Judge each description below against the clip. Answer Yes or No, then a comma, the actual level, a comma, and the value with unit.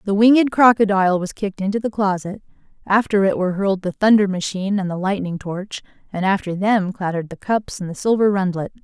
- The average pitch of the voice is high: Yes, high, 195 Hz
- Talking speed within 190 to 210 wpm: Yes, average, 195 wpm